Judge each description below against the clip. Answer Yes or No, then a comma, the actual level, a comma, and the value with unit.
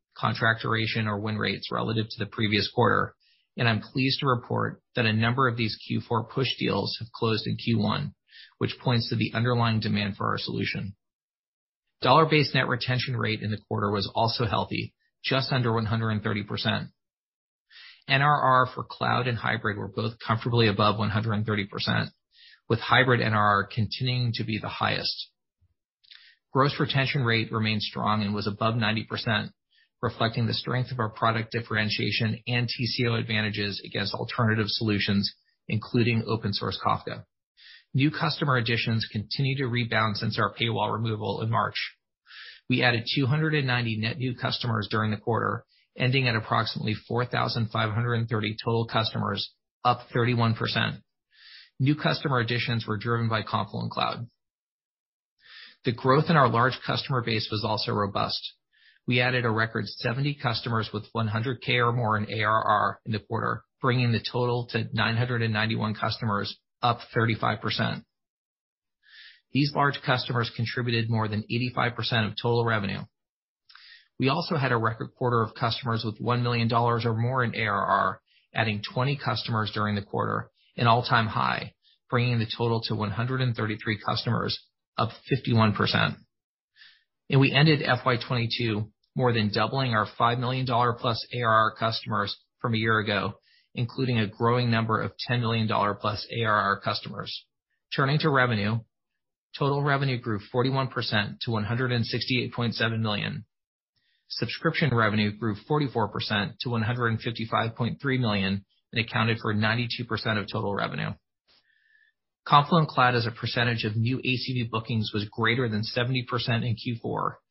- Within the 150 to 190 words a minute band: No, average, 140 wpm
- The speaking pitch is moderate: No, low, 115 Hz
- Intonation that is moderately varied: No, narrow, 2.2 semitones